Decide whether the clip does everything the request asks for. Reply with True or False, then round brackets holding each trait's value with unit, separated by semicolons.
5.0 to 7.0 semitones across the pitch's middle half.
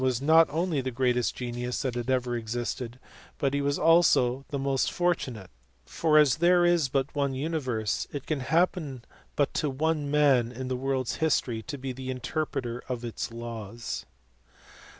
False (3.5 semitones)